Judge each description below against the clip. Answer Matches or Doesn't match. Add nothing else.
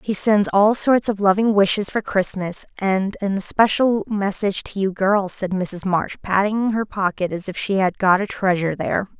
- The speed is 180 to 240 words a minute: Matches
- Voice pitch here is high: Matches